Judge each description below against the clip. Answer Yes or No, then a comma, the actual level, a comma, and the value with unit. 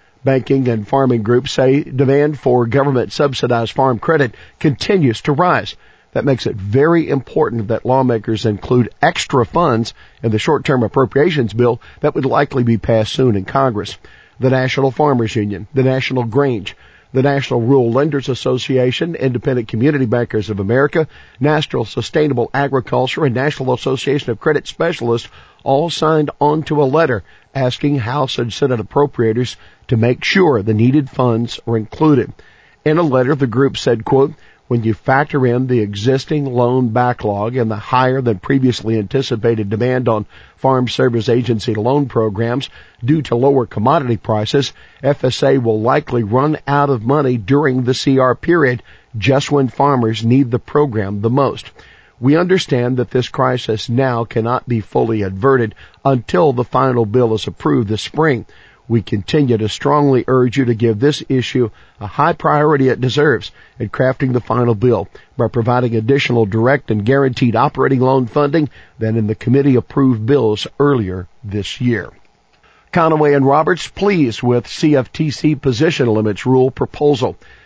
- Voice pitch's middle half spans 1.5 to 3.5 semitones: Yes, average, 3.2 semitones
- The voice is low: Yes, low, 130 Hz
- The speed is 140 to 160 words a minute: Yes, average, 155 wpm